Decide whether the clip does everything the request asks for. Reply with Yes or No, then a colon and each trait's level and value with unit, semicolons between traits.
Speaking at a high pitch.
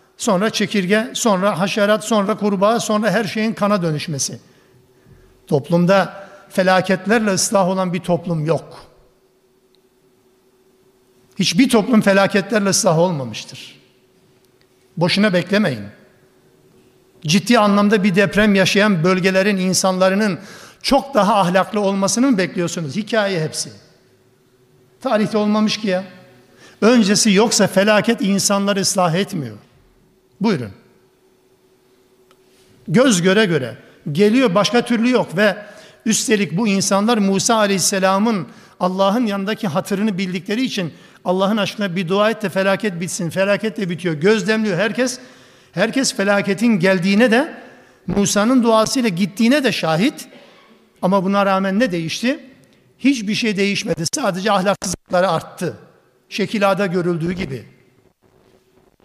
Yes: high, 195 Hz